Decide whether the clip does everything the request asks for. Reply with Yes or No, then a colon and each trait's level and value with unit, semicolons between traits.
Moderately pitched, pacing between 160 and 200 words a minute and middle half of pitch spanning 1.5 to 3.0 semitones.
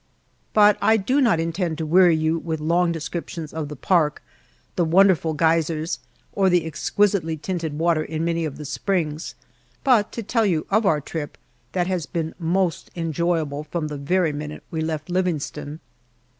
Yes: medium, 165 Hz; average, 170 wpm; average, 2.7 semitones